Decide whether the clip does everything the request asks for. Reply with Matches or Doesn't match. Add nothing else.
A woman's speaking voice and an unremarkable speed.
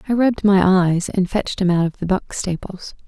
Doesn't match